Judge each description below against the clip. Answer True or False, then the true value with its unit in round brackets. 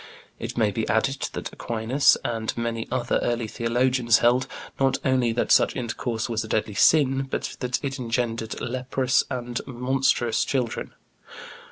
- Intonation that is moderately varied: False (2.2 semitones)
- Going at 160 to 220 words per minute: False (150 wpm)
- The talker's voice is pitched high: False (120 Hz)